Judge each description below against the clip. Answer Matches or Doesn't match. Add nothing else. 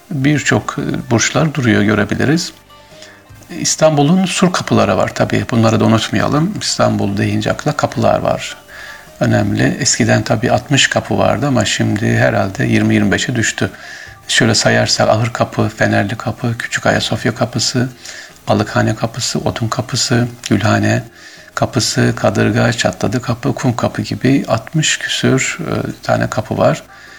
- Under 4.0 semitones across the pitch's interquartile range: Matches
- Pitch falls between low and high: Doesn't match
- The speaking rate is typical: Matches